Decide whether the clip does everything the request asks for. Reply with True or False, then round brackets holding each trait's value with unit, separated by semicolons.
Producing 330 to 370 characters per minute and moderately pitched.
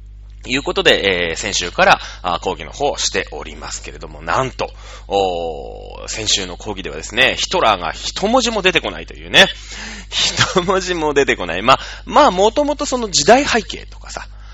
True (350 characters per minute; 145 Hz)